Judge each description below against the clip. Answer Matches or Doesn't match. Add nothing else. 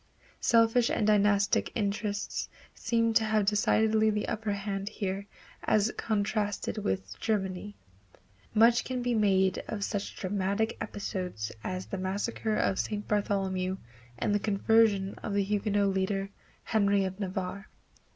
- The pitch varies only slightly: Matches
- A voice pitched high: Matches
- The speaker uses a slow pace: Matches